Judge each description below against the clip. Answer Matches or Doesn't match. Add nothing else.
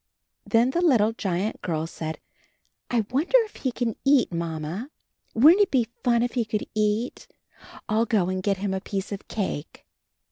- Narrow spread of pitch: Doesn't match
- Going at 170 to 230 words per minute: Matches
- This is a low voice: Doesn't match